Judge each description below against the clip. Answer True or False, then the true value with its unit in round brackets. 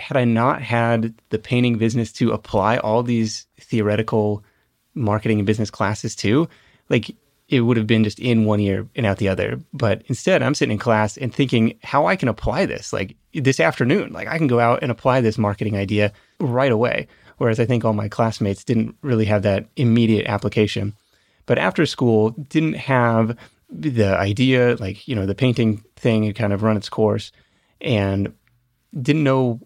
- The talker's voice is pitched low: True (115 Hz)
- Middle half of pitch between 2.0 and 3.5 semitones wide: True (2.6 semitones)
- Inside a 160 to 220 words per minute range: True (185 wpm)